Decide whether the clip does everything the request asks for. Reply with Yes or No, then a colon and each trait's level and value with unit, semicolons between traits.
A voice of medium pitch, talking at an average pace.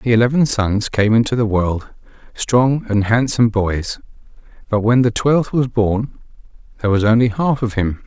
No: low, 115 Hz; average, 170 wpm